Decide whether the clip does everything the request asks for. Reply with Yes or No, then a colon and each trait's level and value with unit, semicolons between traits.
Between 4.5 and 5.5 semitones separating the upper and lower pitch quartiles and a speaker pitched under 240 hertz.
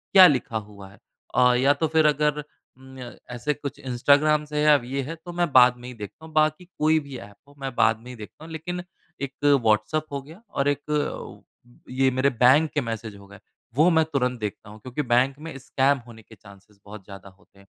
Yes: average, 4.9 semitones; low, 135 Hz